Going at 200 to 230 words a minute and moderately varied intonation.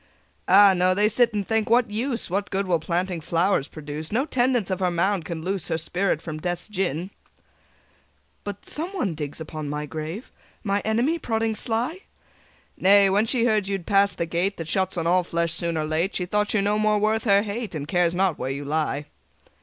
Yes: fast, 205 wpm; average, 4.2 semitones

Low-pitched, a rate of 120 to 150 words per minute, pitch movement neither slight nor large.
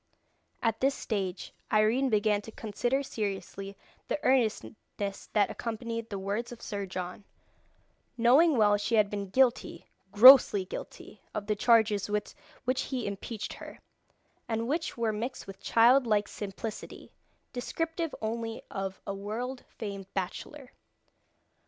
No: high, 220 Hz; slow, 135 wpm; average, 3.3 semitones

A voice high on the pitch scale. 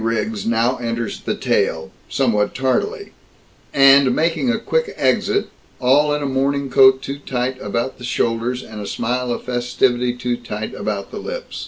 No: low, 125 Hz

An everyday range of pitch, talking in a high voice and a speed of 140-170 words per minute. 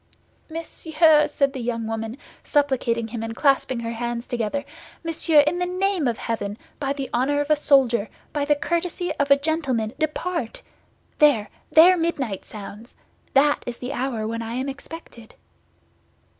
Yes: average, 4.8 semitones; very high, 275 Hz; average, 155 wpm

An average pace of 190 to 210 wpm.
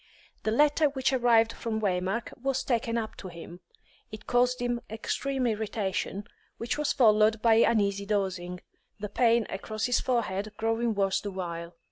No: average, 155 wpm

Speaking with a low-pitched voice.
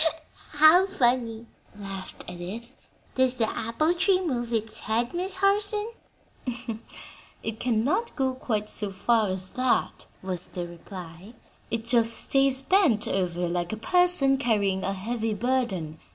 No: high, 230 Hz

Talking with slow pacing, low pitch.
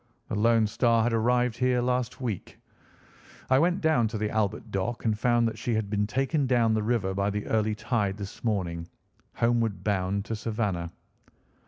No: average, 180 wpm; low, 110 Hz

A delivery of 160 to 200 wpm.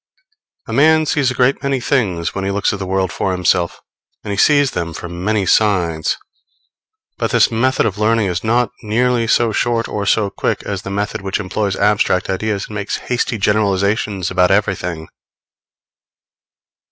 Yes: average, 170 wpm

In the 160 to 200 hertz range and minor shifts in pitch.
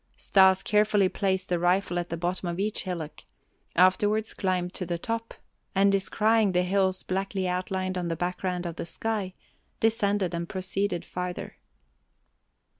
Yes: medium, 185 Hz; narrow, 2.0 semitones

